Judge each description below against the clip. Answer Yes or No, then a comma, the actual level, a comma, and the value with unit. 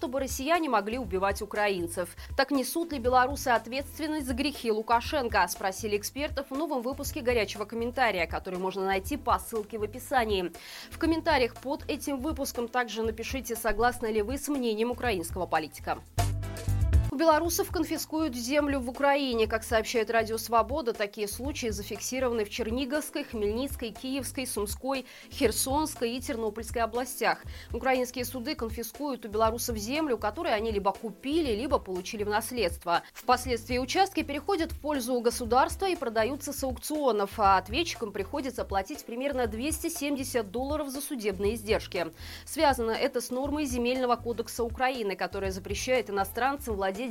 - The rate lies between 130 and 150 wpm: Yes, average, 140 wpm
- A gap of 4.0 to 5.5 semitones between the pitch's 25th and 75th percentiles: Yes, average, 4.3 semitones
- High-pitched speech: Yes, high, 245 Hz